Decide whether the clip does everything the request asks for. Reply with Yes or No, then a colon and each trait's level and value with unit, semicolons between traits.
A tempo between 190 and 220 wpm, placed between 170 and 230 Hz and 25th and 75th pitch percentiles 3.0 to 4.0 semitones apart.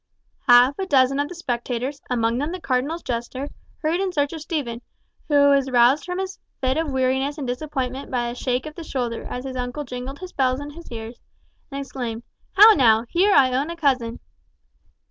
No: average, 200 wpm; very high, 270 Hz; average, 3.5 semitones